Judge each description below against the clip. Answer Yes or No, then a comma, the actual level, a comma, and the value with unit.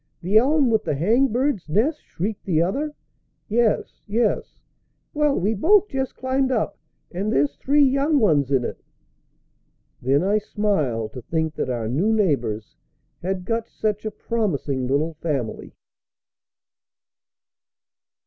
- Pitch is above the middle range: Yes, high, 205 Hz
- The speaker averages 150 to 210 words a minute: No, slow, 135 wpm